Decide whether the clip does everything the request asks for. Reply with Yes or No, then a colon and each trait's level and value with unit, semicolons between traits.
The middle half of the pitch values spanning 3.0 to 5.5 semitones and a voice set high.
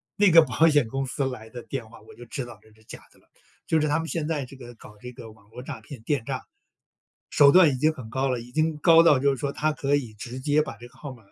No: average, 4.0 semitones; low, 135 Hz